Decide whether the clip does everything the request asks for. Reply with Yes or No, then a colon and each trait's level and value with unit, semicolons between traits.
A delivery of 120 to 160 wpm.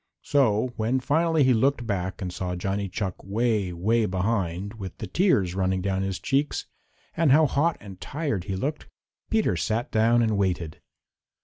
No: average, 170 wpm